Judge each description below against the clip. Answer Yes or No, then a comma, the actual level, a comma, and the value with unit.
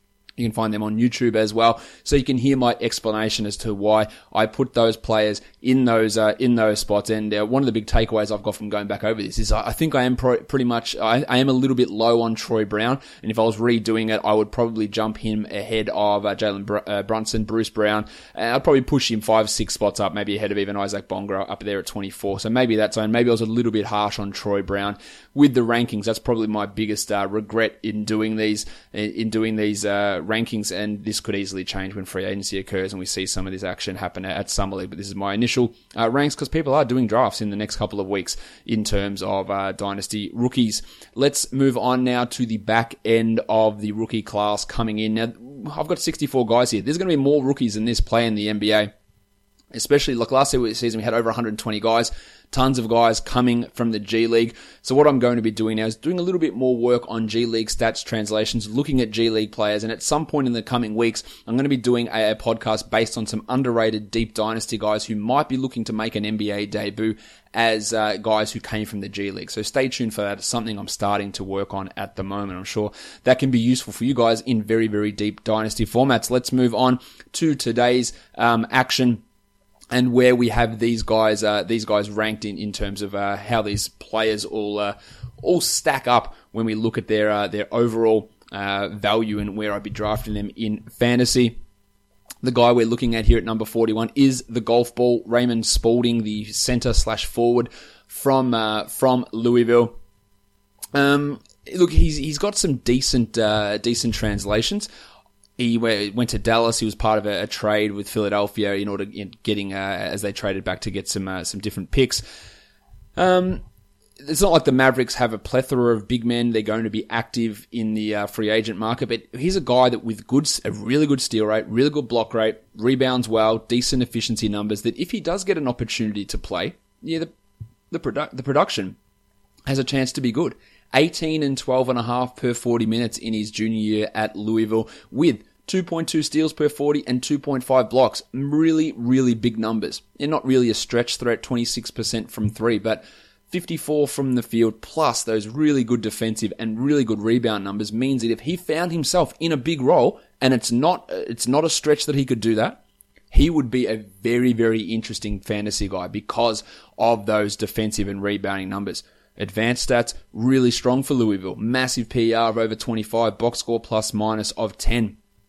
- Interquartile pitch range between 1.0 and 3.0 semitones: Yes, narrow, 2.6 semitones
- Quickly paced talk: Yes, fast, 220 wpm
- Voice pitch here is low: Yes, low, 110 Hz